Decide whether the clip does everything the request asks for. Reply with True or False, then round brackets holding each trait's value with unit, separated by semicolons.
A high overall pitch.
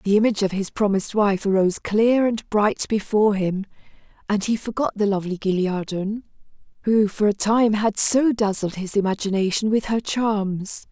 True (210 Hz)